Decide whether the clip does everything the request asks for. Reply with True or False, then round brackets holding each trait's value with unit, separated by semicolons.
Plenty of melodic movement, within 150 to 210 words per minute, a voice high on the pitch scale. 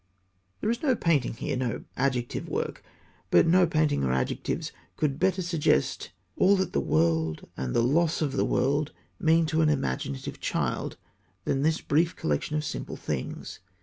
False (6.1 semitones; 170 wpm; 150 Hz)